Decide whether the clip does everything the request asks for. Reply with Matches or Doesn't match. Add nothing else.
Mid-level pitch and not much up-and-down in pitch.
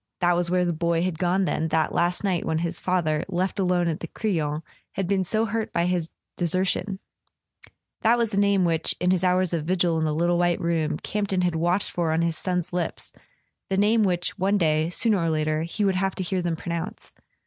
Matches